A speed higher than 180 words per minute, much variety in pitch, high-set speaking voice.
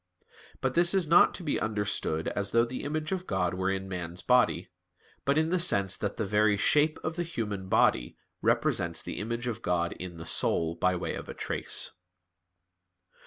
No: average, 190 wpm; wide, 8.5 semitones; low, 105 Hz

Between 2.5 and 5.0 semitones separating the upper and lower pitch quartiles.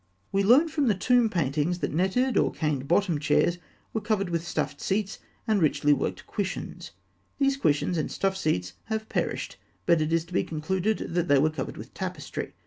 No: wide, 5.4 semitones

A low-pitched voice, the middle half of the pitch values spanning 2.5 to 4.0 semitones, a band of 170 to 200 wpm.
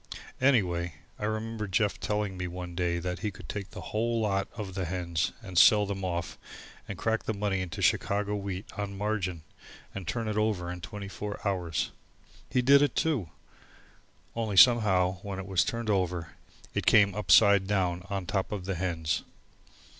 Yes: low, 100 Hz; average, 2.8 semitones; average, 175 wpm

